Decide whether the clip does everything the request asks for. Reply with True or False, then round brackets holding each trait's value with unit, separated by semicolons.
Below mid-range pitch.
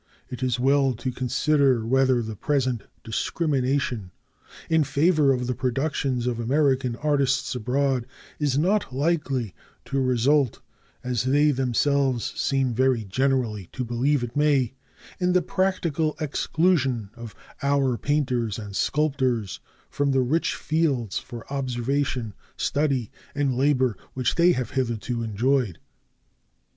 True (130 Hz)